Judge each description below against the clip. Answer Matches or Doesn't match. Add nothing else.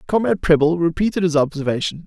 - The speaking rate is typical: Matches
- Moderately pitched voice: Matches